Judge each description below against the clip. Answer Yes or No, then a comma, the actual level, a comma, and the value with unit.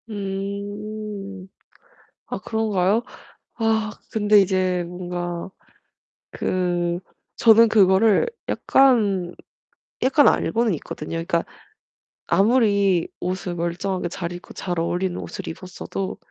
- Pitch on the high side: Yes, high, 195 Hz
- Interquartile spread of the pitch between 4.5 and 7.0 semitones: No, average, 3.2 semitones